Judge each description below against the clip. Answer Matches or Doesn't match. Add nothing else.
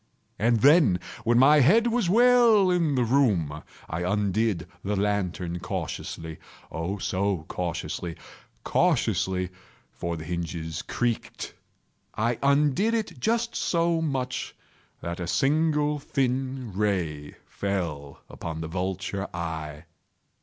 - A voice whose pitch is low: Matches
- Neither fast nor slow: Doesn't match